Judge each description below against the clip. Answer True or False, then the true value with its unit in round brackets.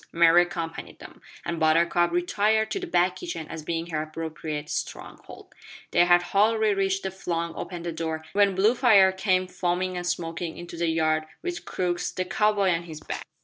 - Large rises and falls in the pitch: False (3.0 semitones)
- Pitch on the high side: False (175 Hz)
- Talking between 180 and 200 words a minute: True (185 wpm)